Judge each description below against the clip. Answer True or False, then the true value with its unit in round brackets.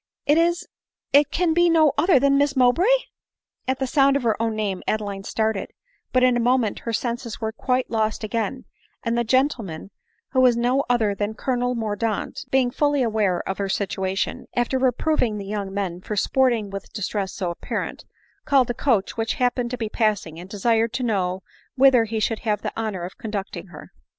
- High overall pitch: True (230 Hz)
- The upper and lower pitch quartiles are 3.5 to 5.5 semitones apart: True (4.0 semitones)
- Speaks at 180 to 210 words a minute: True (195 wpm)